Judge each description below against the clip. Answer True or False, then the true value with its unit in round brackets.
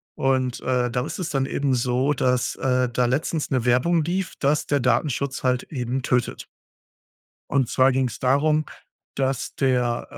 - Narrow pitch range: True (2.1 semitones)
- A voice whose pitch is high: False (130 Hz)